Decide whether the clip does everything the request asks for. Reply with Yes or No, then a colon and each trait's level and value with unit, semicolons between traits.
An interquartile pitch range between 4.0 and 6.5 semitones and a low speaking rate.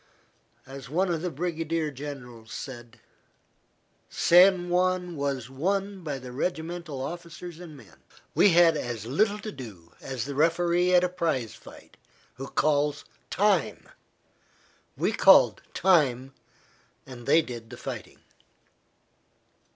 Yes: average, 5.1 semitones; slow, 125 wpm